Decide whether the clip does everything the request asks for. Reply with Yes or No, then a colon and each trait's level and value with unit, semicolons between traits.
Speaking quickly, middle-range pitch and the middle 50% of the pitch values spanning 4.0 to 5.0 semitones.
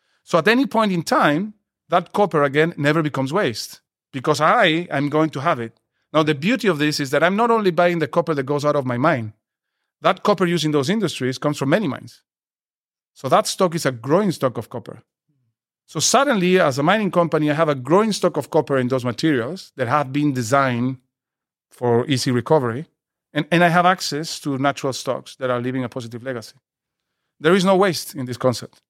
Yes: fast, 210 wpm; medium, 150 Hz; average, 4.6 semitones